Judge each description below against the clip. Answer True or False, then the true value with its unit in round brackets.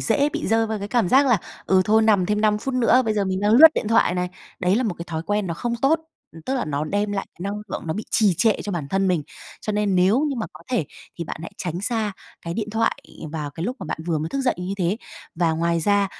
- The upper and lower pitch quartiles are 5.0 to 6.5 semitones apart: False (4.3 semitones)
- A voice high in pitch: True (205 Hz)